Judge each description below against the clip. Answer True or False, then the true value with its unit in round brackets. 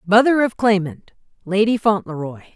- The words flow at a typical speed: False (120 wpm)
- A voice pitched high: True (200 Hz)